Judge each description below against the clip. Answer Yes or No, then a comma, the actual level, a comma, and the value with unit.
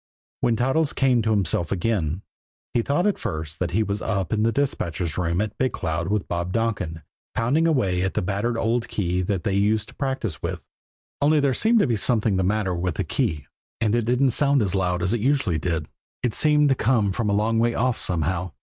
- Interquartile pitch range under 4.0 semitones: No, average, 5.3 semitones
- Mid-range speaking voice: No, low, 105 Hz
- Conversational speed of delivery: No, fast, 215 wpm